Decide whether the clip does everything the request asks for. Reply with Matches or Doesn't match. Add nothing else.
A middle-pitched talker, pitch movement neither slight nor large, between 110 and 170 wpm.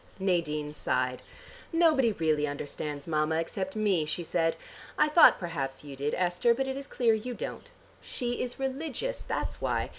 Doesn't match